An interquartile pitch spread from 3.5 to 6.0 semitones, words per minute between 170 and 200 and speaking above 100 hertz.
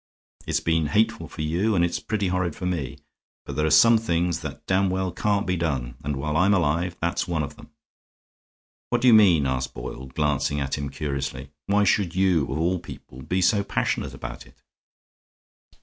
No: average, 4.5 semitones; average, 195 wpm; very low, 85 Hz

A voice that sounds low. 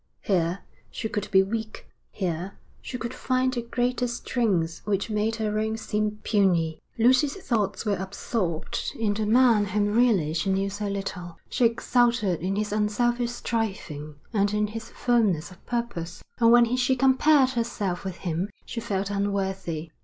No: high, 210 Hz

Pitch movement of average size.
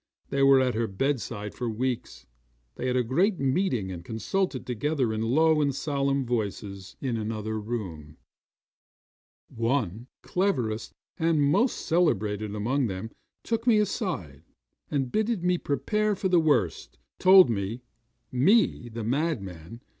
No: wide, 6.8 semitones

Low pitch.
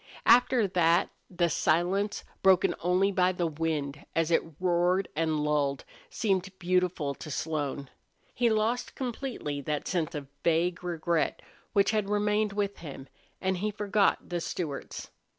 No: medium, 180 Hz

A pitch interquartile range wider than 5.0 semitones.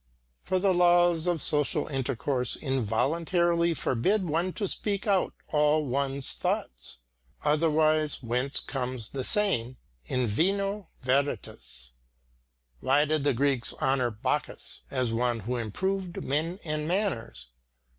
Yes: wide, 5.6 semitones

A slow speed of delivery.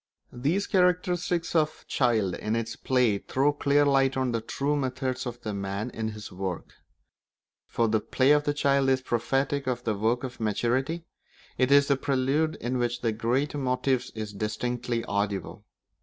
No: average, 170 wpm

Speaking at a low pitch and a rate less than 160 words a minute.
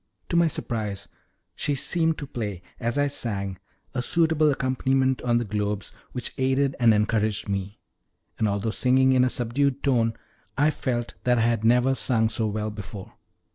No: low, 120 Hz; average, 170 wpm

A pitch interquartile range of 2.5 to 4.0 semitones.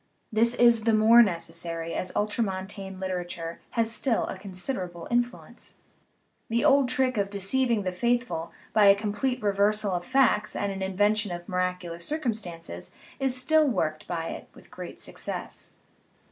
No: average, 4.5 semitones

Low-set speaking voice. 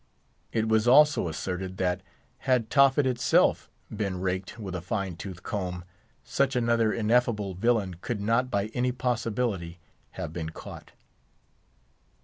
Yes: low, 105 Hz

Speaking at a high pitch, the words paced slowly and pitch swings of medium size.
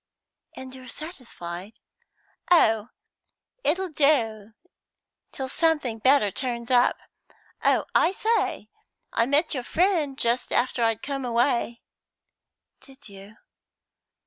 Yes: very high, 255 Hz; slow, 105 wpm; average, 4.5 semitones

